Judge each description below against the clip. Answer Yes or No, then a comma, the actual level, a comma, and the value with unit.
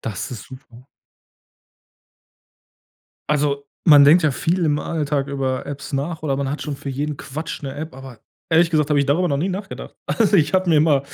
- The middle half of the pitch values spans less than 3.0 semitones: Yes, narrow, 2.6 semitones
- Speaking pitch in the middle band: Yes, medium, 145 Hz